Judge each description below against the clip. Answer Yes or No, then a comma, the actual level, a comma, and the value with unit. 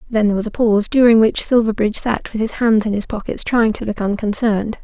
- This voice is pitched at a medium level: No, high, 220 Hz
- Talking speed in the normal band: No, fast, 235 wpm